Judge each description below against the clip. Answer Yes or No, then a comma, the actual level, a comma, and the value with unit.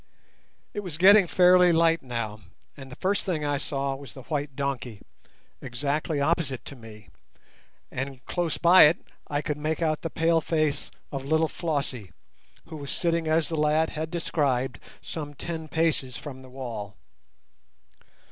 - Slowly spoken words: No, average, 155 wpm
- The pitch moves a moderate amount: Yes, average, 3.5 semitones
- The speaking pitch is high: No, medium, 150 Hz